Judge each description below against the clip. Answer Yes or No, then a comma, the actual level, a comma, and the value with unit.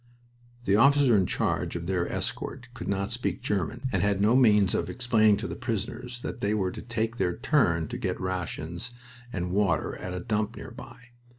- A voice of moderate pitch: No, low, 105 Hz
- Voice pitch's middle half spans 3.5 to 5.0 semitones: Yes, average, 4.6 semitones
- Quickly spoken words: No, average, 190 wpm